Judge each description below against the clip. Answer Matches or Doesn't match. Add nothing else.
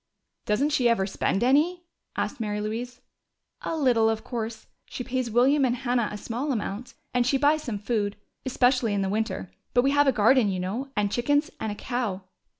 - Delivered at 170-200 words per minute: Matches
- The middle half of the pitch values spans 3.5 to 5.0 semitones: Matches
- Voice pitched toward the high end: Matches